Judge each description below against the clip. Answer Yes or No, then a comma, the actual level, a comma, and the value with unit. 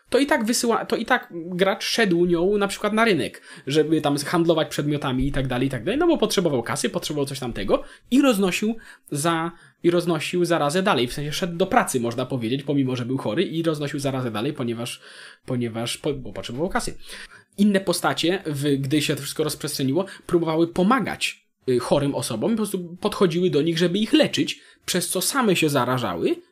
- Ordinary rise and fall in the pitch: No, wide, 5.7 semitones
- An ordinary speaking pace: No, fast, 175 wpm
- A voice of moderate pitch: Yes, medium, 170 Hz